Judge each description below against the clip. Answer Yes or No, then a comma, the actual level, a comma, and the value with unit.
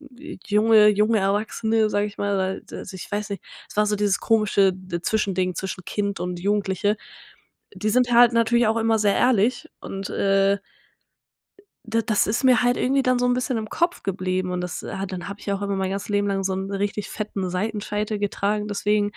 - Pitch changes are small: Yes, narrow, 2.3 semitones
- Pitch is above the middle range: Yes, high, 205 Hz